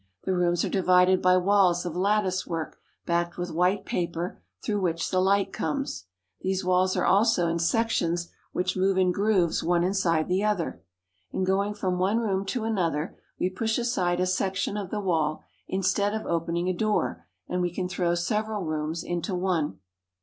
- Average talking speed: Yes, average, 180 wpm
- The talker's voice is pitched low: No, medium, 185 Hz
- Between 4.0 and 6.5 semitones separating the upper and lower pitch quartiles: No, narrow, 2.4 semitones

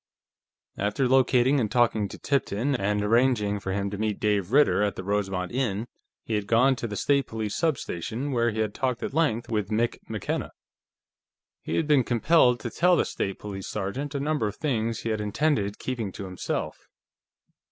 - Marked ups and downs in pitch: No, average, 4.4 semitones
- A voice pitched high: No, low, 115 Hz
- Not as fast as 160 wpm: No, average, 185 wpm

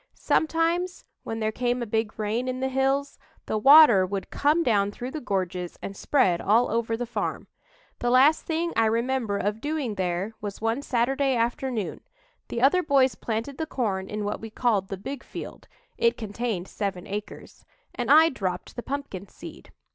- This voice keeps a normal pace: Yes, average, 175 wpm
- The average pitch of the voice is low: No, high, 235 Hz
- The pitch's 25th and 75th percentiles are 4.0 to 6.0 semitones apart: Yes, average, 4.7 semitones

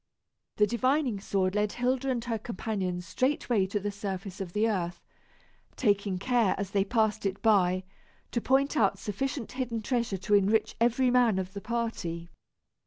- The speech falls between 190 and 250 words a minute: No, average, 165 wpm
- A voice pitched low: No, high, 210 Hz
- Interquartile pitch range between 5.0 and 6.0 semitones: No, average, 3.7 semitones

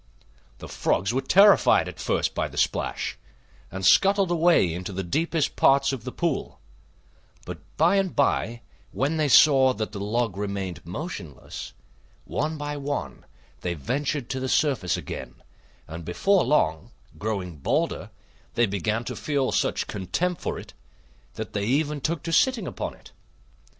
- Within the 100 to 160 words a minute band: Yes, average, 155 wpm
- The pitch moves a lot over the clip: Yes, wide, 7.9 semitones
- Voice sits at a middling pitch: No, low, 130 Hz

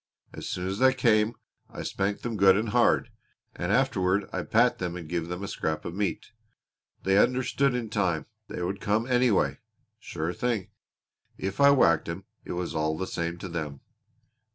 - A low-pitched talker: Yes, very low, 95 Hz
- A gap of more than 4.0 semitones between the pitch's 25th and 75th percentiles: Yes, average, 4.6 semitones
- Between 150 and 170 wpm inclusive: No, average, 180 wpm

